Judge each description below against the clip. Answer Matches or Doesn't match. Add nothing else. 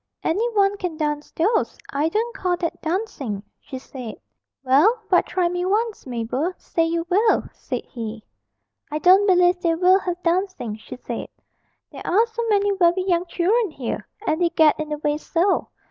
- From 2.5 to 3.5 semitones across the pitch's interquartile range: Doesn't match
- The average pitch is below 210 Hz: Doesn't match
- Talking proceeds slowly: Doesn't match